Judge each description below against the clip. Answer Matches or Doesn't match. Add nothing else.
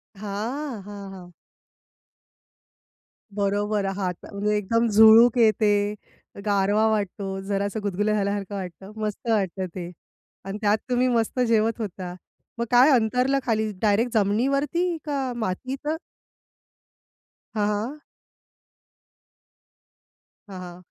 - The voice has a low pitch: Doesn't match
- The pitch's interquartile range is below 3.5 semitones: Matches